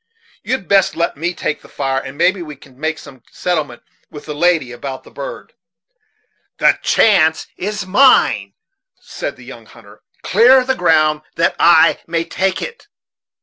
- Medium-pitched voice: Yes, medium, 165 Hz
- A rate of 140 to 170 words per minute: Yes, average, 160 wpm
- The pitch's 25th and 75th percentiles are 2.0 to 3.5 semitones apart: No, average, 4.7 semitones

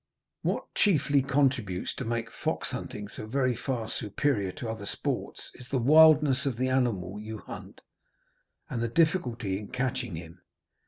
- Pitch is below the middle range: Yes, low, 120 Hz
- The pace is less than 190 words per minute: Yes, average, 155 wpm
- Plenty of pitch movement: No, average, 4.3 semitones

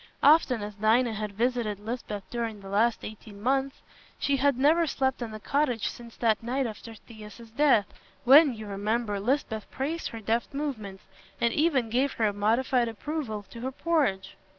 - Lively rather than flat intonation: No, average, 4.0 semitones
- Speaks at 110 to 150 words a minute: No, average, 170 wpm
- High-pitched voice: Yes, high, 235 Hz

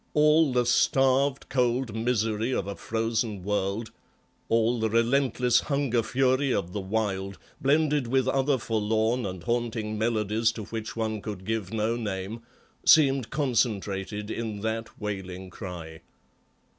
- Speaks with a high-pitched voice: No, low, 115 Hz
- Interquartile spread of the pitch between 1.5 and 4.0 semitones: Yes, average, 3.3 semitones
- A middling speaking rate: No, slow, 130 wpm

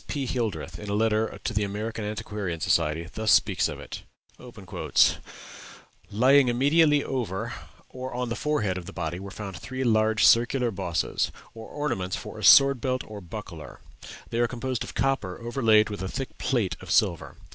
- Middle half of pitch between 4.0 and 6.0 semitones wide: Yes, average, 4.7 semitones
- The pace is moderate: Yes, average, 170 wpm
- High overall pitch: No, low, 110 Hz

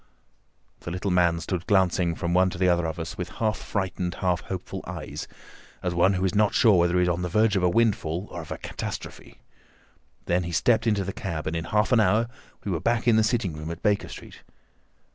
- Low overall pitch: Yes, very low, 90 Hz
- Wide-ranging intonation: No, average, 3.3 semitones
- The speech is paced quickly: Yes, fast, 230 wpm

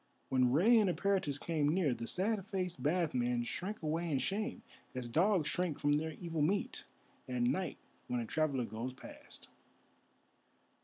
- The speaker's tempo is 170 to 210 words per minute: No, average, 160 wpm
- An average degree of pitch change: No, wide, 6.4 semitones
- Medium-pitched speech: Yes, medium, 160 Hz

